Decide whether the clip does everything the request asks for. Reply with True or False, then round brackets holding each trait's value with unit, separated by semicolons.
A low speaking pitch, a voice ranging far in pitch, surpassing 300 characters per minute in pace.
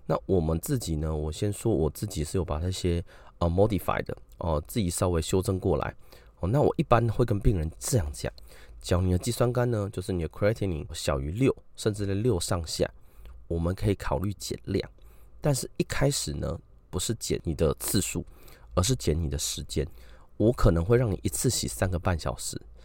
False (95 Hz; 4.9 semitones; 315 characters per minute)